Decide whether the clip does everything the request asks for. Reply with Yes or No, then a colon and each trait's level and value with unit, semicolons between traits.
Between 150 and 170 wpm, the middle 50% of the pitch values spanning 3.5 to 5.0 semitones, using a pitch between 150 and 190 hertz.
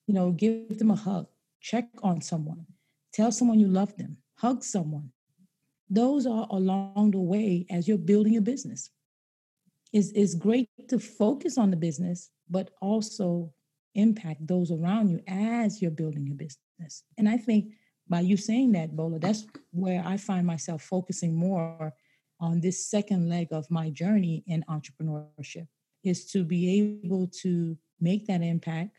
Yes: average, 165 wpm; average, 4.0 semitones; medium, 185 Hz